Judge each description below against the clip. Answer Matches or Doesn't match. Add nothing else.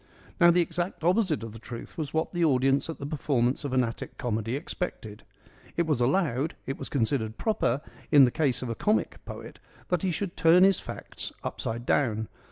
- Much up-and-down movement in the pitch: Matches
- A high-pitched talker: Doesn't match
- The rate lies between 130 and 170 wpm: Doesn't match